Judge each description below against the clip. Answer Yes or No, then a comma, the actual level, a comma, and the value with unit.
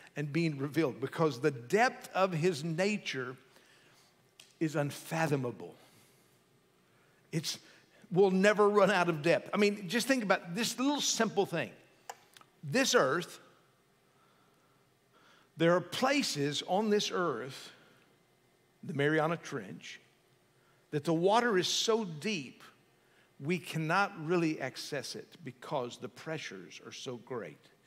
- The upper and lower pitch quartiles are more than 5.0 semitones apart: Yes, wide, 5.5 semitones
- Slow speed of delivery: Yes, slow, 120 wpm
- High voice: No, medium, 170 Hz